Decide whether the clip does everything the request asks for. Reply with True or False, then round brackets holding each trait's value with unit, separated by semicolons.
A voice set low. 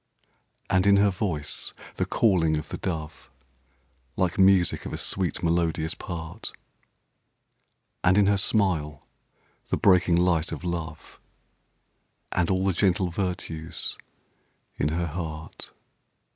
True (85 Hz)